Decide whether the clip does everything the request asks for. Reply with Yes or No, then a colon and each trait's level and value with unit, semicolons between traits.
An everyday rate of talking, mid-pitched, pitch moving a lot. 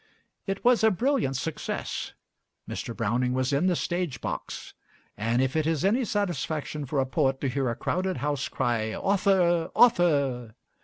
Yes: average, 160 wpm; medium, 155 Hz; wide, 6.2 semitones